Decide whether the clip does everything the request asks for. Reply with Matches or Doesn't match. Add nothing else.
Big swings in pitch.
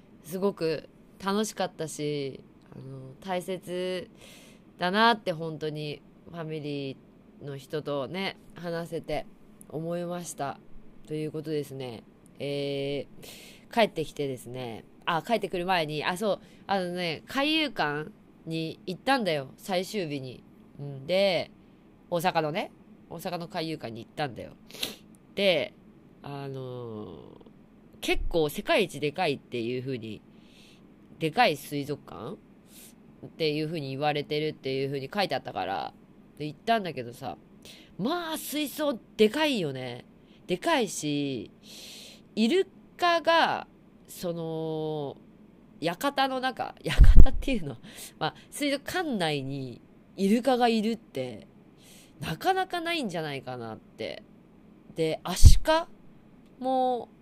Matches